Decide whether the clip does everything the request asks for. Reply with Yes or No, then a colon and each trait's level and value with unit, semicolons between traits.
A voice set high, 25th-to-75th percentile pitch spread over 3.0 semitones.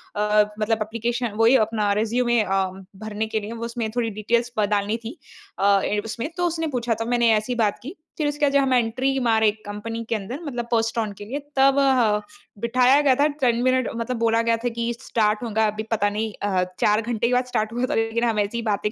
No: high, 230 Hz; narrow, 2.5 semitones